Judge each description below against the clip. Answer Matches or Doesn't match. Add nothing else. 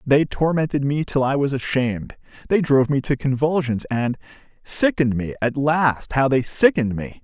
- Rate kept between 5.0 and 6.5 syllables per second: Matches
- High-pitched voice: Doesn't match